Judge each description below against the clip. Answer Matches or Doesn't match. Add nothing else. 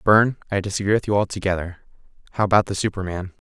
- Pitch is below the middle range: Matches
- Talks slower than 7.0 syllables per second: Doesn't match